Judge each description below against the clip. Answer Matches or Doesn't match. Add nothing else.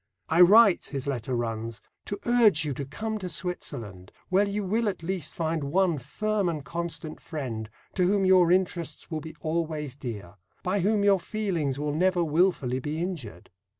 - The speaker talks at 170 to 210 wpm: Matches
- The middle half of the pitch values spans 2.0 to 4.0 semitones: Doesn't match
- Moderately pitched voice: Matches